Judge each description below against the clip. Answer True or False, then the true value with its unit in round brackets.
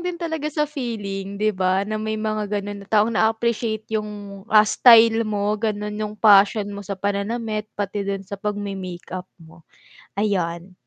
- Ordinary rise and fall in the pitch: False (1.8 semitones)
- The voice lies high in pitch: True (210 Hz)